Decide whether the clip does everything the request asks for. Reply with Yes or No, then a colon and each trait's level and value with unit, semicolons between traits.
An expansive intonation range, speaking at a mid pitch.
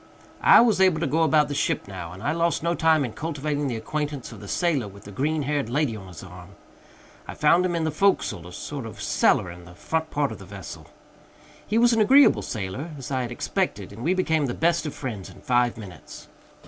Yes: wide, 7.7 semitones; medium, 145 Hz